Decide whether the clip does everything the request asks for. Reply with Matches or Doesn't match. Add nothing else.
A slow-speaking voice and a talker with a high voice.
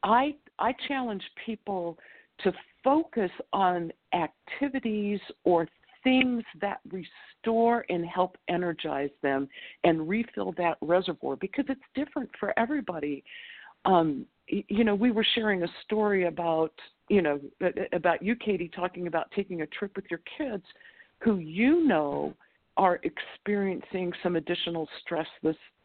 Matches